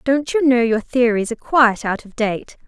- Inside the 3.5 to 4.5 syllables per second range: No, 5.2 syllables/s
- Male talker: No, female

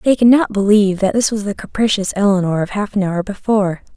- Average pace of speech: No, fast, 225 wpm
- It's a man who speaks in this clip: No, female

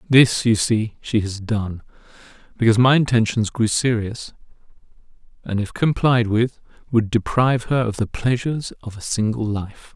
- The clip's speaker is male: Yes, male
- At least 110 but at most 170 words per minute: Yes, average, 150 wpm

